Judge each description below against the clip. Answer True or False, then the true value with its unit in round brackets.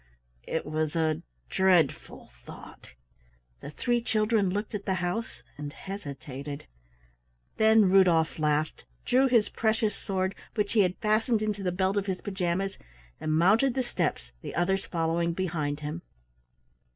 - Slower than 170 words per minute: True (140 wpm)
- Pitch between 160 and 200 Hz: True (190 Hz)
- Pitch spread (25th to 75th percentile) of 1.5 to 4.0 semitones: False (4.7 semitones)